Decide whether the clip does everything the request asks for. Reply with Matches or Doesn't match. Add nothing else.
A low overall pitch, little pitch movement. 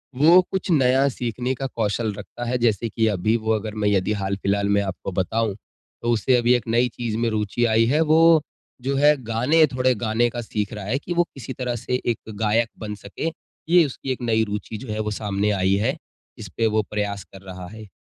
Doesn't match